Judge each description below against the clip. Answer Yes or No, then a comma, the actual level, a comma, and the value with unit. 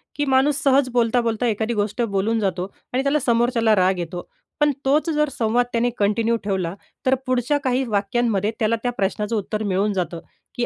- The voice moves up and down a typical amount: Yes, average, 3.7 semitones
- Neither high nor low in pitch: No, high, 230 Hz